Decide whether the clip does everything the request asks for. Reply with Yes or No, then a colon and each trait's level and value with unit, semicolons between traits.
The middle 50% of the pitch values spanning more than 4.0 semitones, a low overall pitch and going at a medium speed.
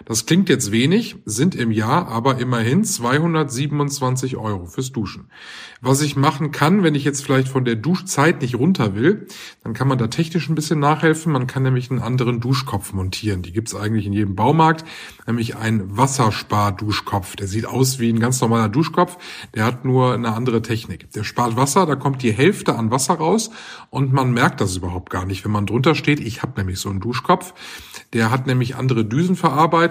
No: wide, 5.5 semitones; low, 130 Hz; fast, 200 wpm